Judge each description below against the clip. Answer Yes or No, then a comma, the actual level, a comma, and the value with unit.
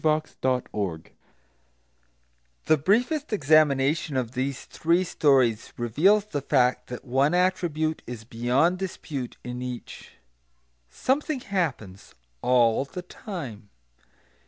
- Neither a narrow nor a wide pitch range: No, wide, 6.6 semitones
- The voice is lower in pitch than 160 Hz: Yes, low, 135 Hz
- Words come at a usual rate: No, slow, 95 wpm